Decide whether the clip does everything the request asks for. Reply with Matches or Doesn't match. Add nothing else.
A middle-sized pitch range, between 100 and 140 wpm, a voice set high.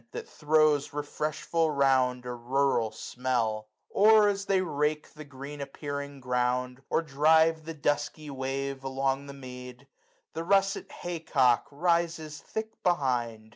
Doesn't match